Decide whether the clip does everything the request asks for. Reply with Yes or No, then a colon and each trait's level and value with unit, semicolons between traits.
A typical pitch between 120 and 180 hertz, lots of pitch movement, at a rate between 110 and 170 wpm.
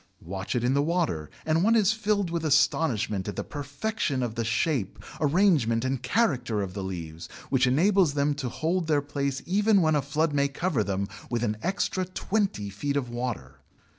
No: medium, 140 Hz; wide, 6.7 semitones; average, 190 wpm